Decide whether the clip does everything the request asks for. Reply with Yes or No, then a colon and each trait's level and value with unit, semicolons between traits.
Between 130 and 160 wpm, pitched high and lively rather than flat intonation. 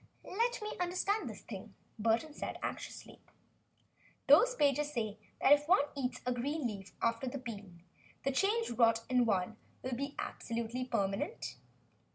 No: average, 150 wpm; very high, 250 Hz; average, 4.8 semitones